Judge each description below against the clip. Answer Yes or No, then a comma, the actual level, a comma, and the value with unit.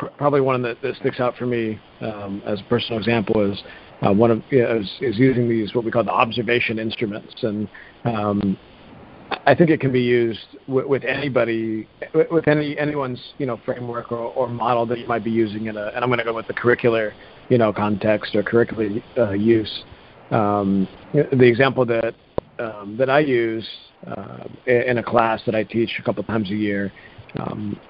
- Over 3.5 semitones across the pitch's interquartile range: No, narrow, 2.5 semitones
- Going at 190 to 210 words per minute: Yes, average, 195 wpm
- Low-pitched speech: Yes, low, 115 Hz